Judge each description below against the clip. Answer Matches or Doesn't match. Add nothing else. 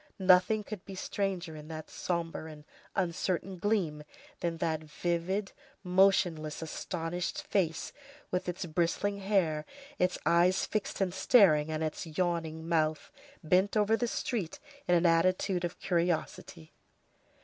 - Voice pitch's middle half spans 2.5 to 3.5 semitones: Matches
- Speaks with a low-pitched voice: Doesn't match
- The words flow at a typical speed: Doesn't match